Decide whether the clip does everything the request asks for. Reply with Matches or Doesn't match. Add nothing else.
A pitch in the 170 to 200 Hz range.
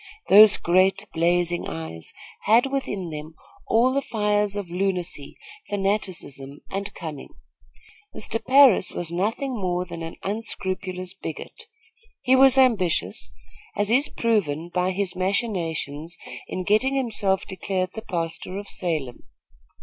Matches